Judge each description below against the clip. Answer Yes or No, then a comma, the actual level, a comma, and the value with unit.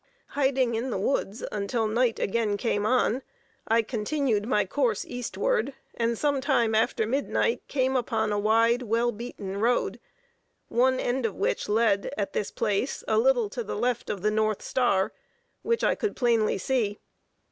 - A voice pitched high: Yes, high, 230 Hz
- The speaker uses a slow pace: No, average, 165 wpm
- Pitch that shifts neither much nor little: Yes, average, 3.5 semitones